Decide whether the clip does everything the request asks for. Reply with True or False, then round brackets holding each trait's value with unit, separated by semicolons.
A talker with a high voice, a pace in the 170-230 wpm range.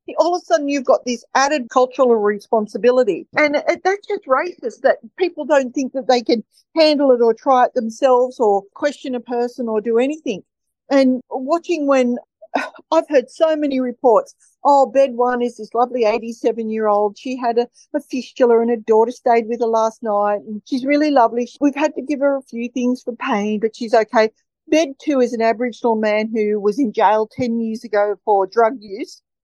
True (250 Hz; 200 wpm)